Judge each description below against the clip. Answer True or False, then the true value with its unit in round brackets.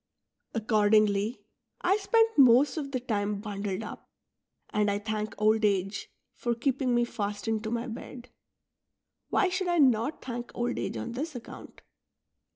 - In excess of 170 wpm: False (150 wpm)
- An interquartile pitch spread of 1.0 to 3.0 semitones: False (3.5 semitones)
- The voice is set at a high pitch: True (230 Hz)